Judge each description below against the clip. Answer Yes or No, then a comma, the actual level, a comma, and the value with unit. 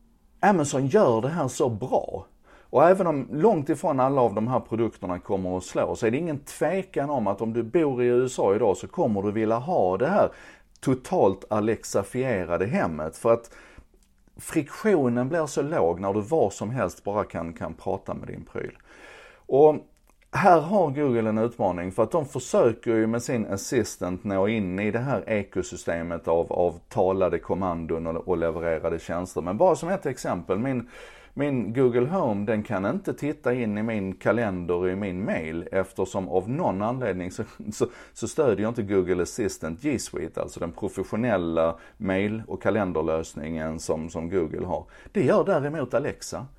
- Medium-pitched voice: No, low, 110 Hz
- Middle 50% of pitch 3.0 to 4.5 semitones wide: No, average, 5.3 semitones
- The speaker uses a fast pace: No, average, 175 wpm